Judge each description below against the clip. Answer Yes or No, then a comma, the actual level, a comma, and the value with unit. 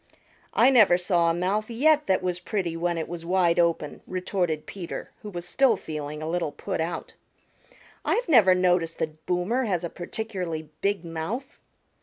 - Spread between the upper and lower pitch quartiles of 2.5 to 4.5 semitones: Yes, average, 3.5 semitones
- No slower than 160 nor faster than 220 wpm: Yes, average, 170 wpm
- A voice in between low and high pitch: Yes, medium, 180 Hz